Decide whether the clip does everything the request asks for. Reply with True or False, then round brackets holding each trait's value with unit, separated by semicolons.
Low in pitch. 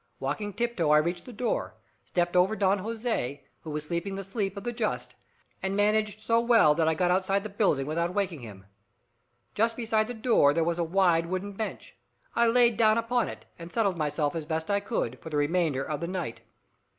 False (190 Hz)